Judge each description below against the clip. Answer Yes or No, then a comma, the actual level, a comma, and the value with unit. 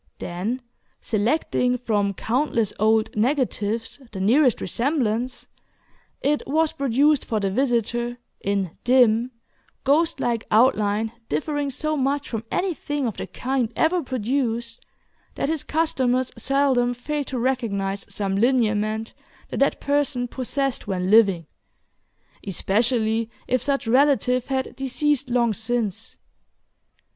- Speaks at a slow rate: Yes, slow, 115 wpm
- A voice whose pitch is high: Yes, high, 245 Hz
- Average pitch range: Yes, average, 4.0 semitones